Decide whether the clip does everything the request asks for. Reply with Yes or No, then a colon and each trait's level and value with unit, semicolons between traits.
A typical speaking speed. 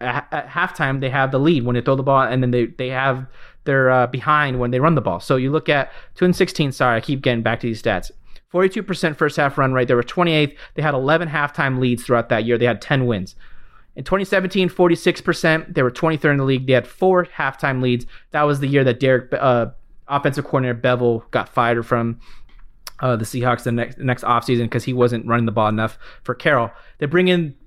No: fast, 225 wpm